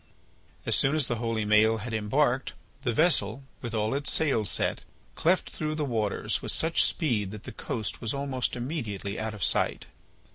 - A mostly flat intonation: No, average, 4.7 semitones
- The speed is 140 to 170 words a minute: No, average, 180 wpm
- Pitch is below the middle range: Yes, low, 120 Hz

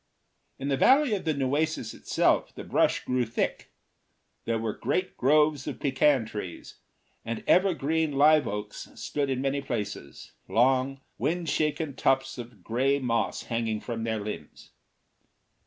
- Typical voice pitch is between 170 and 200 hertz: No, low, 135 Hz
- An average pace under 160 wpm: Yes, average, 145 wpm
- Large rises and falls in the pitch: No, average, 4.6 semitones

